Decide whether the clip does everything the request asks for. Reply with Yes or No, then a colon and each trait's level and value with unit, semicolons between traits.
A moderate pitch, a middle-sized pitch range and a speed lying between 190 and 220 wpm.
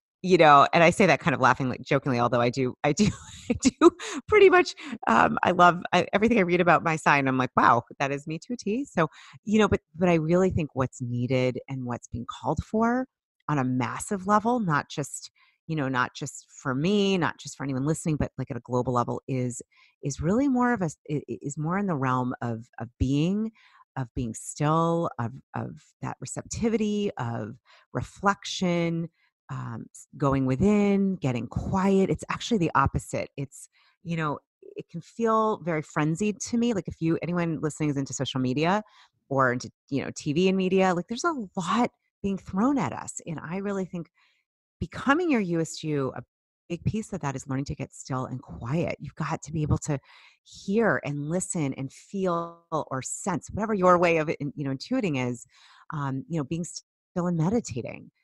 No: medium, 160 Hz; wide, 6.5 semitones; average, 195 wpm